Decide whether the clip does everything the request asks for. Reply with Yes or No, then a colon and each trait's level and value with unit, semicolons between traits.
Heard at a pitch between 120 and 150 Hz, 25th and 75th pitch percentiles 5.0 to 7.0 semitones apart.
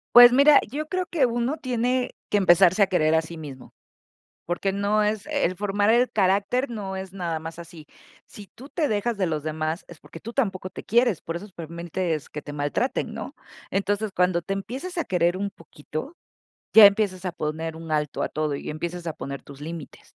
No: high, 190 Hz; average, 5.3 semitones